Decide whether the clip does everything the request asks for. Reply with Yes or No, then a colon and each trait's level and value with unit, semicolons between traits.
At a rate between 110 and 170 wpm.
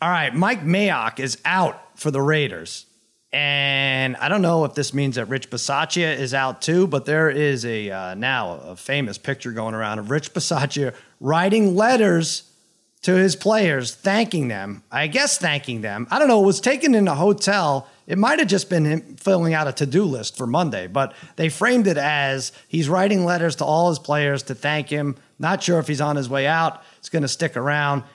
No: fast, 205 wpm